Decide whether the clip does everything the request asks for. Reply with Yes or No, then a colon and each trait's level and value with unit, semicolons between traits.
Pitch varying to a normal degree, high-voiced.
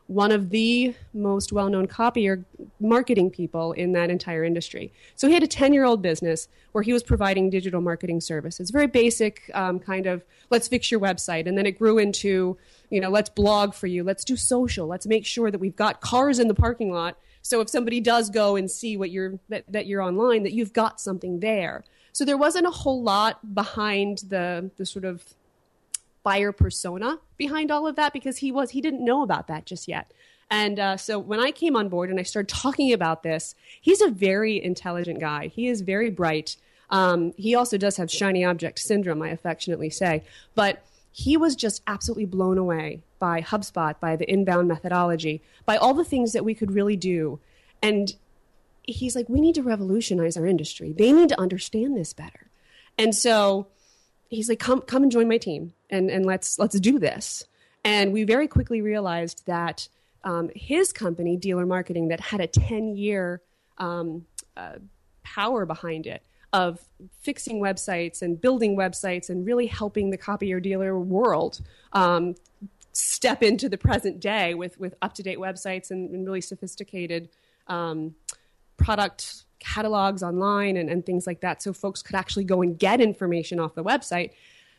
Yes: average, 4.0 semitones; high, 195 Hz